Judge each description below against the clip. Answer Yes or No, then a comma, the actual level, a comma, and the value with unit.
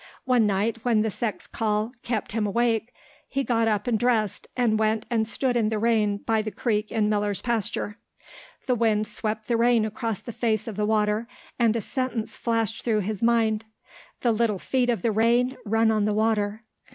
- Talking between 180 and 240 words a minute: Yes, average, 195 wpm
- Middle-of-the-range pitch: No, high, 220 Hz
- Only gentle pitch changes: Yes, narrow, 1.7 semitones